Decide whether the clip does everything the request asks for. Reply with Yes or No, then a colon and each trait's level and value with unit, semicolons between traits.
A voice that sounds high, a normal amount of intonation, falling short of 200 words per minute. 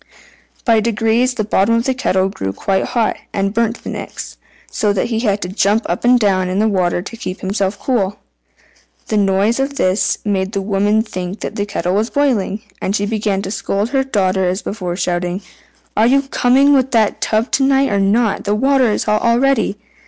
No: high, 210 Hz; average, 3.3 semitones; fast, 205 wpm